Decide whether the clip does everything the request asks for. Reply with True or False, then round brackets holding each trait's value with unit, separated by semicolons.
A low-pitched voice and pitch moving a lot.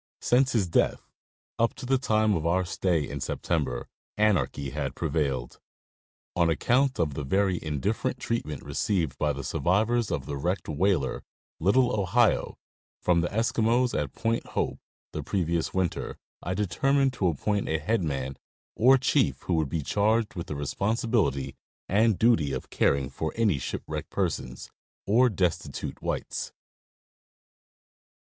True (95 Hz; 7.2 semitones)